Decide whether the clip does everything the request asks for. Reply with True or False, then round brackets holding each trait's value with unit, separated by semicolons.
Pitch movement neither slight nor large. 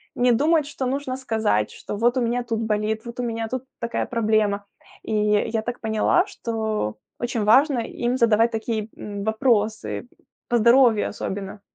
False (2.3 semitones)